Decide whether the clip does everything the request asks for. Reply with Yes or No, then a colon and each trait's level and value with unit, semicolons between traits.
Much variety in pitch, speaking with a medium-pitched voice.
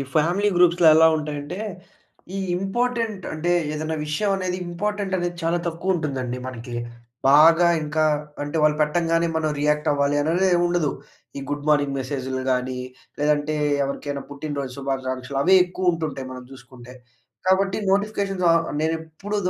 No: average, 3.9 semitones; medium, 155 Hz